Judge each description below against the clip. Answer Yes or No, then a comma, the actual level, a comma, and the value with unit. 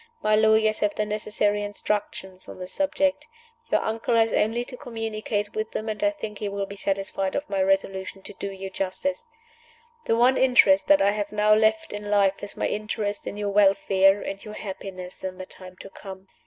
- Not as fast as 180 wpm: No, average, 200 wpm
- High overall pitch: Yes, high, 205 Hz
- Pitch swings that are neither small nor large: No, narrow, 2.0 semitones